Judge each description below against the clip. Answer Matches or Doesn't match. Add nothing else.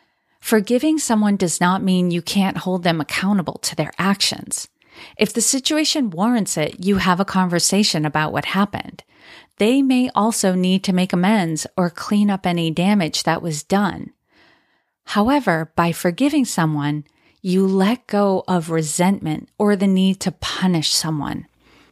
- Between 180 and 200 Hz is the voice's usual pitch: Matches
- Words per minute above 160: Doesn't match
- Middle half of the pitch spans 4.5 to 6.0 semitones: Doesn't match